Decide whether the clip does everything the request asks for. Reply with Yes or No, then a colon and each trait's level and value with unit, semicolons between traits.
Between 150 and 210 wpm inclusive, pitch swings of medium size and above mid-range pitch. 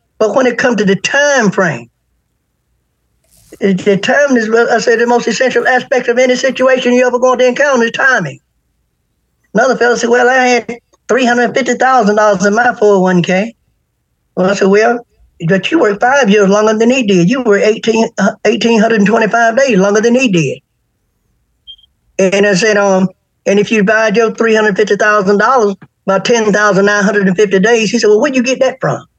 Yes: average, 165 wpm; average, 3.3 semitones; high, 220 Hz